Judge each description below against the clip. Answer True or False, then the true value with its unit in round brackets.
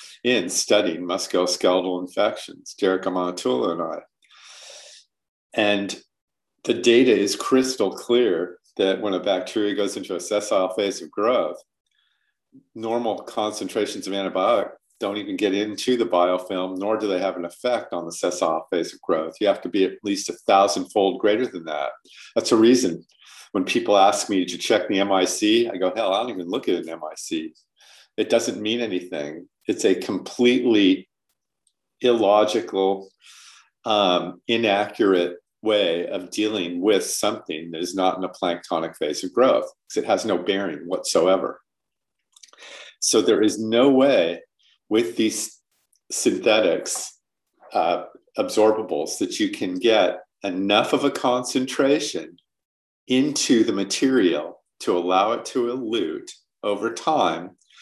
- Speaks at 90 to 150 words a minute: True (145 wpm)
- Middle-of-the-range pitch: False (110 Hz)